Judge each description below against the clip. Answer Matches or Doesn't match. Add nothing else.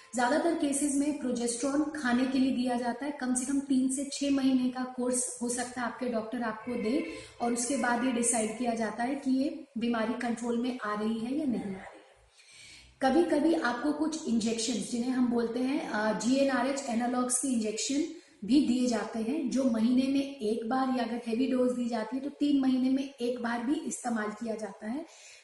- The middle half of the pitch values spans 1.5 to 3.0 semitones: Matches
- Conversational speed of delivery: Doesn't match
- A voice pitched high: Matches